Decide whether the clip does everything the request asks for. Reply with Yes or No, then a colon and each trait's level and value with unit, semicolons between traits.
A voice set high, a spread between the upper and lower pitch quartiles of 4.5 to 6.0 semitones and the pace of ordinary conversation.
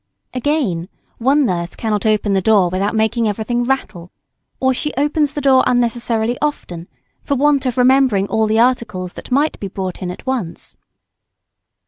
Yes: high, 230 Hz; average, 5.1 semitones; average, 160 wpm